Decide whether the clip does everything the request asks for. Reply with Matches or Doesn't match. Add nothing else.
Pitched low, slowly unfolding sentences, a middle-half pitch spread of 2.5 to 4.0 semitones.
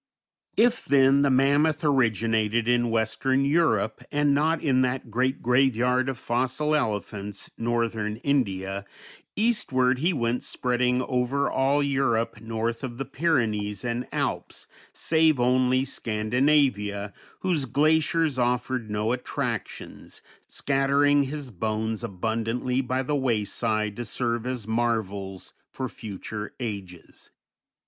Matches